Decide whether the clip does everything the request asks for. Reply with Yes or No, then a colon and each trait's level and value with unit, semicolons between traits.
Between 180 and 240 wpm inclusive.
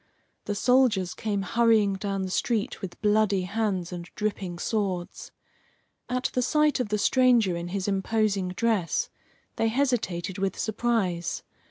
No: average, 140 wpm